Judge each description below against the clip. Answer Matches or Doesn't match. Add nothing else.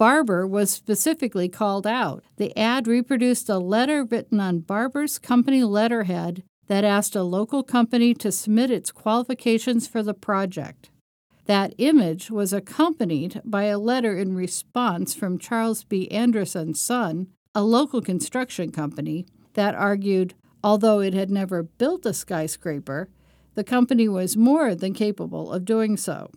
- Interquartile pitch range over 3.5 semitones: Matches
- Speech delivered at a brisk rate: Doesn't match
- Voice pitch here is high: Matches